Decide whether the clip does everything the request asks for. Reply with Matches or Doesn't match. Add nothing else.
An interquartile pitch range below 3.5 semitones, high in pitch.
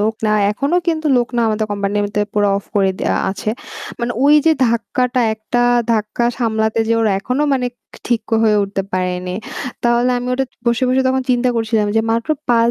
Matches